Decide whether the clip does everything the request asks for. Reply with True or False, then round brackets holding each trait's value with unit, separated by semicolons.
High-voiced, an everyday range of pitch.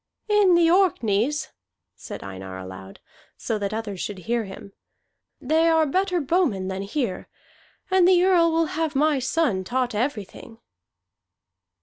False (260 Hz; 8.9 semitones)